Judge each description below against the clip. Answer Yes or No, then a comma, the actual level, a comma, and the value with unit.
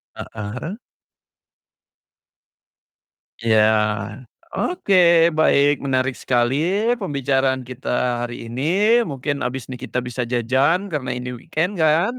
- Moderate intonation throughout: Yes, average, 3.6 semitones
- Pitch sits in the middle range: No, low, 130 Hz